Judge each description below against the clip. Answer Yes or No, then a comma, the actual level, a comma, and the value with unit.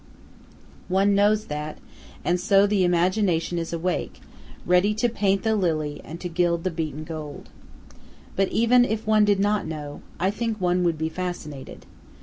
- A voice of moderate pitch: Yes, medium, 180 Hz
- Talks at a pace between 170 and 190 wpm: No, average, 160 wpm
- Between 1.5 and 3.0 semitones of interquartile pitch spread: No, average, 4.0 semitones